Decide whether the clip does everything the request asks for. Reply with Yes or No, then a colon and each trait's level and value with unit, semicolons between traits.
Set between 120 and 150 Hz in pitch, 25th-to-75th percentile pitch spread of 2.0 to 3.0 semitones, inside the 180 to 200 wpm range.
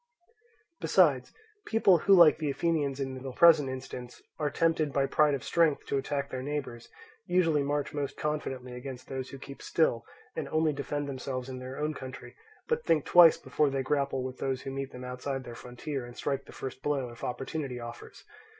Yes: medium, 140 Hz; narrow, 2.6 semitones; average, 190 wpm